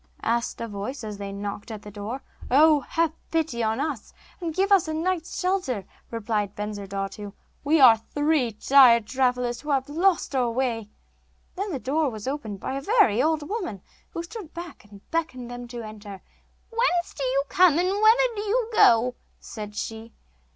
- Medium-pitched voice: No, very high, 260 Hz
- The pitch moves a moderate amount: No, wide, 7.0 semitones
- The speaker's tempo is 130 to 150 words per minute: No, average, 180 wpm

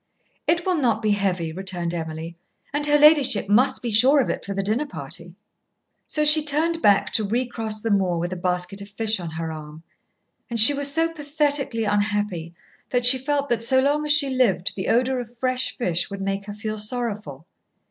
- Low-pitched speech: No, high, 220 Hz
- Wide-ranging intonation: Yes, wide, 6.2 semitones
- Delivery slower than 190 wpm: No, average, 200 wpm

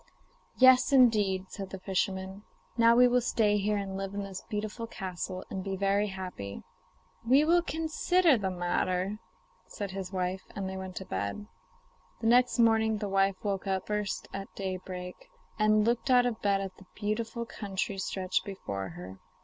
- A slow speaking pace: No, average, 175 wpm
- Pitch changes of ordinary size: Yes, average, 3.0 semitones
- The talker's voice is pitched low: No, high, 195 Hz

